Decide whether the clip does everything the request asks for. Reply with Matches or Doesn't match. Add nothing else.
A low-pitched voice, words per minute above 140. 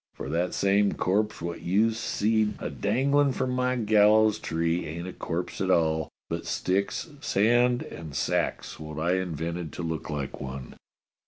Matches